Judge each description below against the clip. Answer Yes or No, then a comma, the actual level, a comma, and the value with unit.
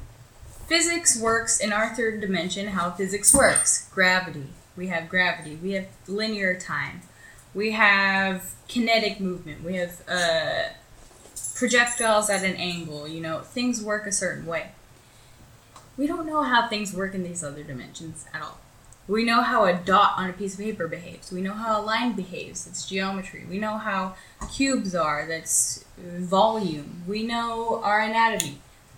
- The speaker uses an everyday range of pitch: Yes, average, 4.4 semitones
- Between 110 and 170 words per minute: Yes, average, 160 wpm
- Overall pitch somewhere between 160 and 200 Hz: Yes, high, 190 Hz